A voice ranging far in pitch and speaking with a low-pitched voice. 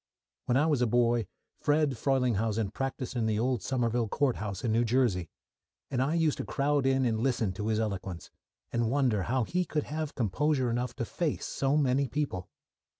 No: average, 3.8 semitones; low, 125 Hz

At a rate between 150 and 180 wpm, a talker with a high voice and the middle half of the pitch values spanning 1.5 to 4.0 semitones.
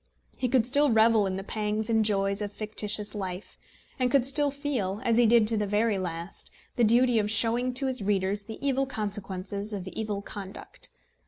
No: average, 190 wpm; high, 215 Hz; average, 3.1 semitones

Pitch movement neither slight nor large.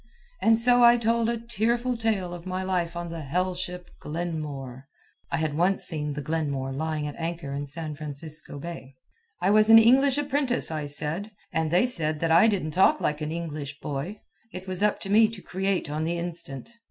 No: wide, 5.7 semitones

